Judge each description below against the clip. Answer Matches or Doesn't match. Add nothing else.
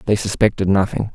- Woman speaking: Doesn't match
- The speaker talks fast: Doesn't match